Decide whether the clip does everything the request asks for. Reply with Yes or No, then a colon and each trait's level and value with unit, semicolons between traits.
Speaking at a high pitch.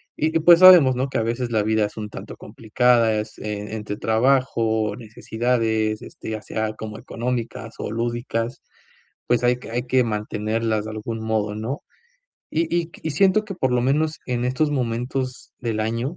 No: low, 115 Hz